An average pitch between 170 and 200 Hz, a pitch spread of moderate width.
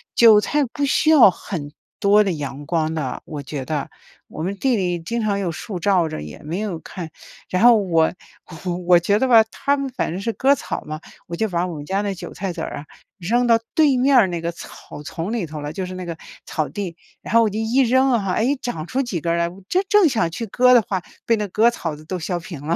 No: high, 190 Hz; wide, 5.9 semitones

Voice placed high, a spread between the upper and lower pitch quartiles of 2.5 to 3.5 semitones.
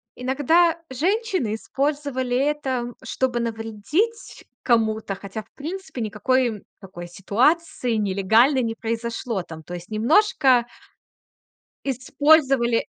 No: high, 245 Hz; average, 4.8 semitones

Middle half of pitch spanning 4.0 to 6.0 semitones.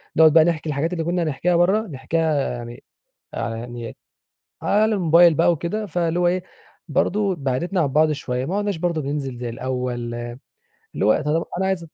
Yes: average, 4.7 semitones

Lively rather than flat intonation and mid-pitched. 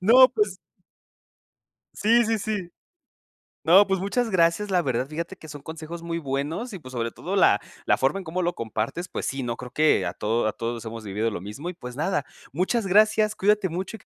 Yes: wide, 7.4 semitones; medium, 170 Hz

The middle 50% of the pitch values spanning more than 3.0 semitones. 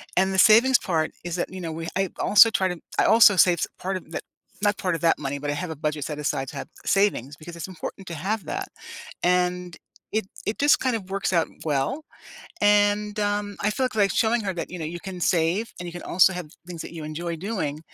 Yes: average, 3.9 semitones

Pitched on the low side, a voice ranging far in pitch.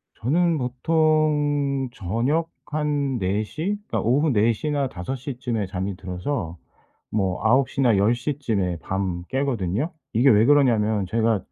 Yes: low, 125 Hz; wide, 6.0 semitones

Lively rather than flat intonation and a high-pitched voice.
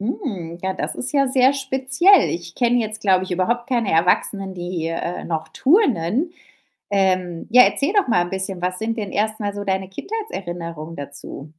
Yes: wide, 6.1 semitones; high, 195 Hz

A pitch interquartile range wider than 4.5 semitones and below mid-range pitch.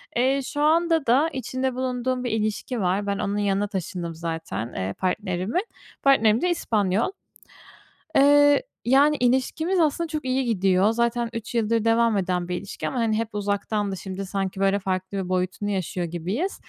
No: average, 5.3 semitones; high, 215 Hz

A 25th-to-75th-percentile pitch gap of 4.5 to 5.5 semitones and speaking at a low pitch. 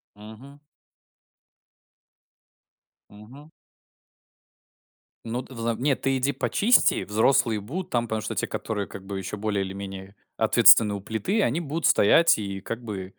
Yes: average, 5.0 semitones; low, 110 Hz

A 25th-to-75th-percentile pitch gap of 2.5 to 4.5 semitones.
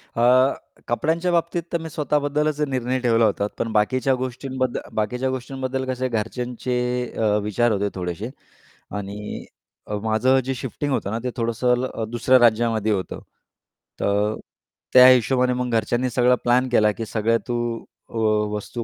Yes: average, 2.8 semitones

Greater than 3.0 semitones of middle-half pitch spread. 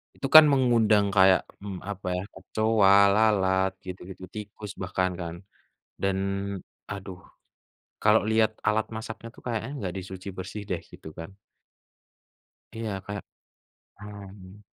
No: narrow, 2.6 semitones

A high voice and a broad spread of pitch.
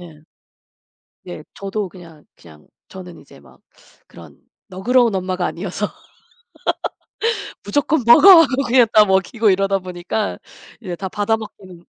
No: high, 195 Hz; average, 3.6 semitones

